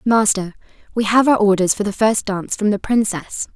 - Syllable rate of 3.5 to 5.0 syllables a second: No, 5.3 syllables/s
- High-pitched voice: Yes, high, 210 Hz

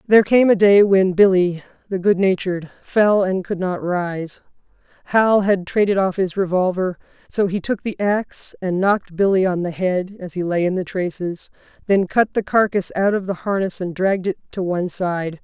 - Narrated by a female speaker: Yes, female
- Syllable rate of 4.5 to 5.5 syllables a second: Yes, 5.0 syllables/s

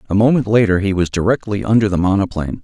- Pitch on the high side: No, low, 100 Hz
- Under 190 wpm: No, fast, 205 wpm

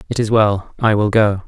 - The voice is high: No, low, 105 Hz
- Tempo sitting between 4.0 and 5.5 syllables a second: Yes, 5.3 syllables/s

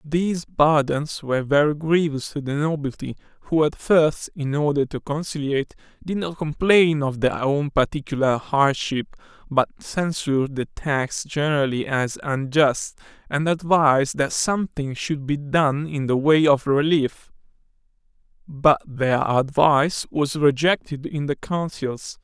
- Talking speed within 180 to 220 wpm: No, slow, 135 wpm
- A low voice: No, medium, 145 Hz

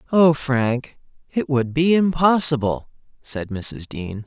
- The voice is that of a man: Yes, male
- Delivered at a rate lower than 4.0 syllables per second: Yes, 3.5 syllables/s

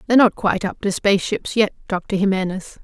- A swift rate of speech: No, average, 190 wpm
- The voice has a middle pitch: No, high, 195 Hz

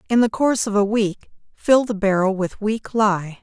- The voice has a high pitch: Yes, high, 210 Hz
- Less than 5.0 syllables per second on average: Yes, 4.7 syllables/s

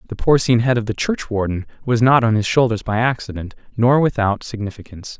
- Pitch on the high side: No, low, 115 Hz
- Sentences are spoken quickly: No, average, 185 wpm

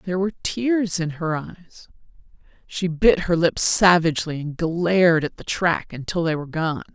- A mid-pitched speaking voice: Yes, medium, 170 Hz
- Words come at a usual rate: Yes, average, 165 wpm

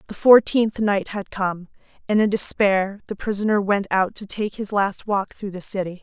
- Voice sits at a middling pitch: No, high, 200 Hz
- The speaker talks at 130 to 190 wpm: No, average, 200 wpm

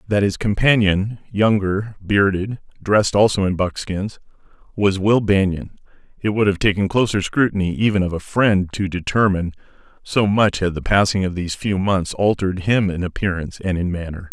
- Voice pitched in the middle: No, low, 100 Hz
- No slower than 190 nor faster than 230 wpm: No, average, 170 wpm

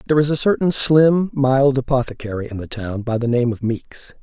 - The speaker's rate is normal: No, fast, 215 wpm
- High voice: No, low, 130 Hz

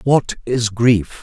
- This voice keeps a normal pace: Yes, average, 145 wpm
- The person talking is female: No, male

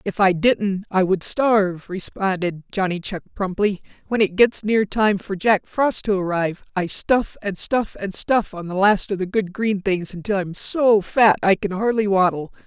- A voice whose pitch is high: Yes, high, 200 Hz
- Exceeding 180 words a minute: Yes, average, 200 wpm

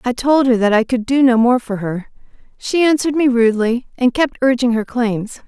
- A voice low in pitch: No, high, 245 Hz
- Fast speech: Yes, fast, 220 wpm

